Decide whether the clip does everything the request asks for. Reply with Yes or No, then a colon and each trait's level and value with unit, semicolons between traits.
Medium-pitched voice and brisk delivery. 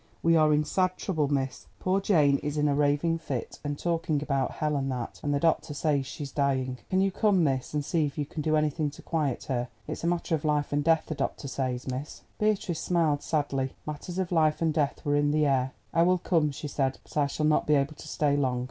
Yes: medium, 150 Hz; fast, 245 wpm